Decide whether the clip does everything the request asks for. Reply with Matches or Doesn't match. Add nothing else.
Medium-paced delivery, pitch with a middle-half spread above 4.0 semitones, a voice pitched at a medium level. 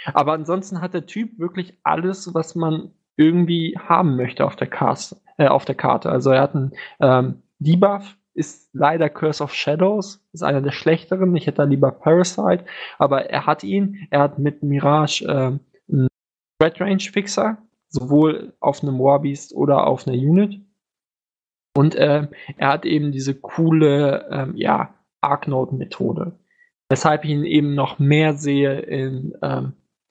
Matches